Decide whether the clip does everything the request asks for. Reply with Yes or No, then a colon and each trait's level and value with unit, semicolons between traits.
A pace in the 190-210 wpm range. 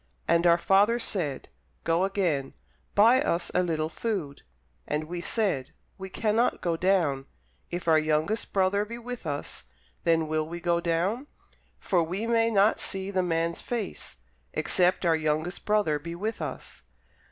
No: average, 155 wpm